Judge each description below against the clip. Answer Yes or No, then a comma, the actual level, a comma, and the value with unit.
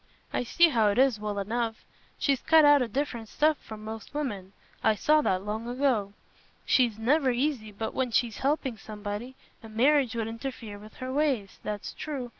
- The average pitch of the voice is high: Yes, high, 235 Hz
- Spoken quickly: No, average, 180 wpm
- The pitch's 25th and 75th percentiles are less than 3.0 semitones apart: No, average, 4.2 semitones